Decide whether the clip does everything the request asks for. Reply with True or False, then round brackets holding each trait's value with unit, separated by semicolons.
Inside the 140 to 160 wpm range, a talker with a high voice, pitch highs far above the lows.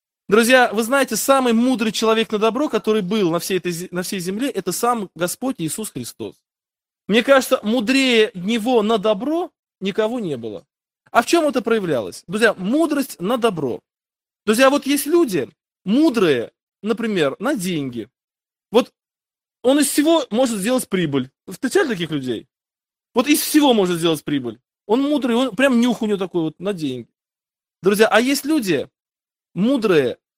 True (155 wpm; 225 Hz; 5.9 semitones)